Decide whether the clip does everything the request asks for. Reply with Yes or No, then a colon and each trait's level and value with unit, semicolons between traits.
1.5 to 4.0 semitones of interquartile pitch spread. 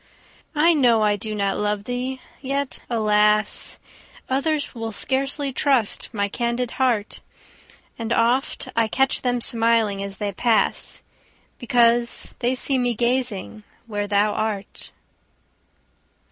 Yes: average, 3.5 semitones